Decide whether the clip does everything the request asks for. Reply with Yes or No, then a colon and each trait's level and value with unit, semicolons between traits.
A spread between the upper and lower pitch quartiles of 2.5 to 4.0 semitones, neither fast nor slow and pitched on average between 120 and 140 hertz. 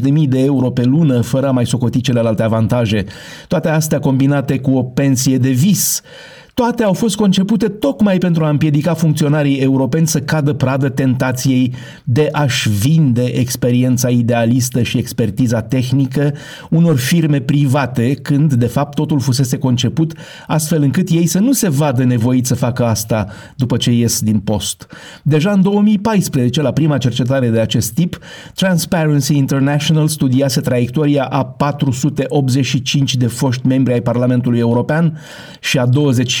Yes: average, 3.6 semitones; average, 150 wpm; low, 135 Hz